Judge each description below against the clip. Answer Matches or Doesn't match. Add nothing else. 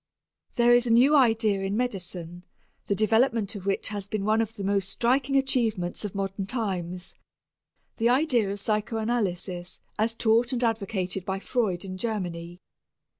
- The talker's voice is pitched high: Matches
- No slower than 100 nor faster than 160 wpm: Matches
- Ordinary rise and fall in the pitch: Matches